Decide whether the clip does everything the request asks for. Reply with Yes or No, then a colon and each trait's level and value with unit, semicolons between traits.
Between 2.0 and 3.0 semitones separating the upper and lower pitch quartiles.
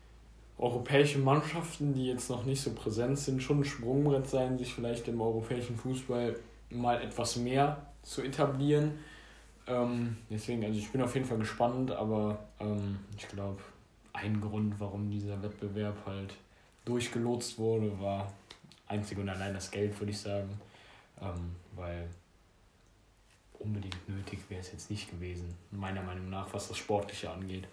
No: average, 3.7 semitones